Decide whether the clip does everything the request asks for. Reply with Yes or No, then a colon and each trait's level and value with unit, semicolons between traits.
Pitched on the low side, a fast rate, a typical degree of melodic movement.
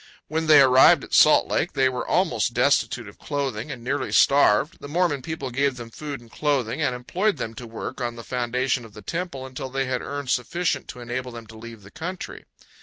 Yes: low, 130 Hz; fast, 215 wpm; average, 3.3 semitones